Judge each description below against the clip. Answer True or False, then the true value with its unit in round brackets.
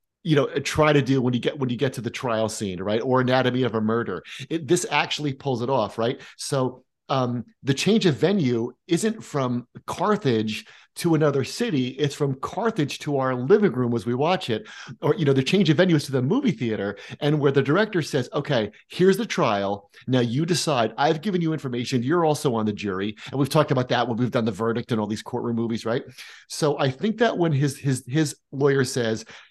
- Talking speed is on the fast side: True (225 wpm)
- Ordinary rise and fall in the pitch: True (4.2 semitones)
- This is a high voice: False (135 Hz)